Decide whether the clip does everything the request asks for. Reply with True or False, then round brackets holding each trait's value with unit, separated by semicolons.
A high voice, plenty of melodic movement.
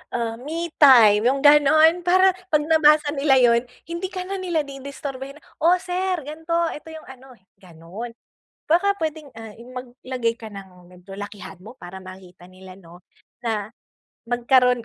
True (260 Hz; 6.4 semitones)